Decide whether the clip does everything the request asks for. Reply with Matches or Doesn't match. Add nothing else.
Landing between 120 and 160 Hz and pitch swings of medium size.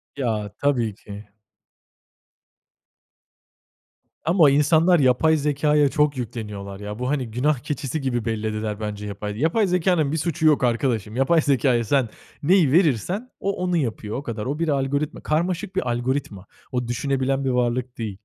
Matches